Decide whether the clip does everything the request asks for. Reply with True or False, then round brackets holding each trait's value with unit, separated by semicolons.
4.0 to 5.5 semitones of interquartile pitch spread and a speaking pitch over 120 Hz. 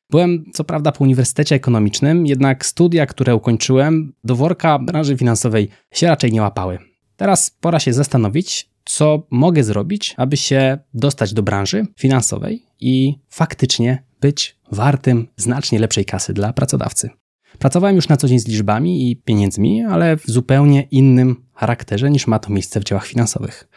True (4.7 semitones; 130 Hz)